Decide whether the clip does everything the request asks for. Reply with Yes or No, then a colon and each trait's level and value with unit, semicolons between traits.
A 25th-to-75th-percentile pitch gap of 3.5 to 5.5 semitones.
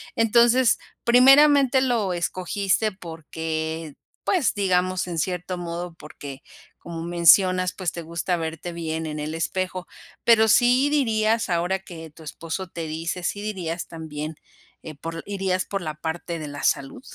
Yes: average, 4.0 semitones